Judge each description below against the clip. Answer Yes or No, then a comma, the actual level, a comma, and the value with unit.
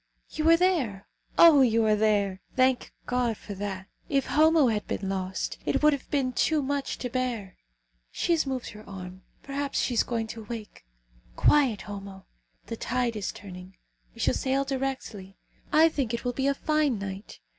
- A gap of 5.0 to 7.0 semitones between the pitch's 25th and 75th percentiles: Yes, wide, 5.4 semitones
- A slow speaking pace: No, average, 180 wpm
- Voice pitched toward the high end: Yes, high, 240 Hz